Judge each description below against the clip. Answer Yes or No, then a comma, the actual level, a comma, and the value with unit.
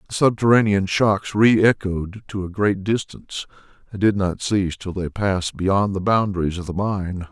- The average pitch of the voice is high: No, low, 100 Hz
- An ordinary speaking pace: Yes, average, 180 wpm